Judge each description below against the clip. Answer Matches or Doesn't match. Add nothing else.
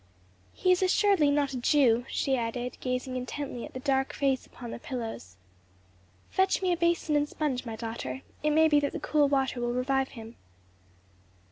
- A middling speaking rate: Matches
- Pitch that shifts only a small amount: Doesn't match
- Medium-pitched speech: Doesn't match